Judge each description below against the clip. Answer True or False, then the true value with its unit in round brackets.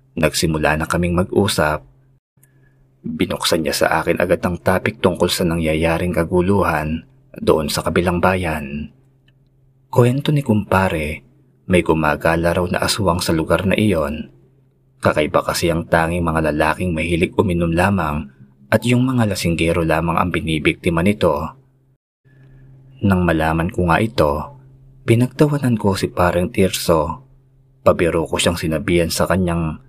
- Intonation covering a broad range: True (7.9 semitones)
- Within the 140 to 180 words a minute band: False (130 wpm)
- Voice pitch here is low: True (90 Hz)